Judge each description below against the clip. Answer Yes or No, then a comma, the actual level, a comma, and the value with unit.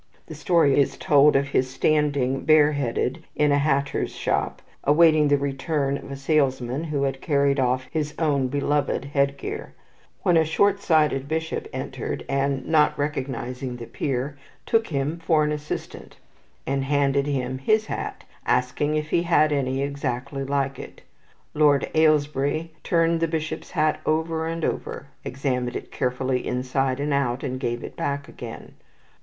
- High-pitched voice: No, medium, 140 Hz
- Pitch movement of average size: No, narrow, 2.3 semitones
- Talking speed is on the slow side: No, average, 160 wpm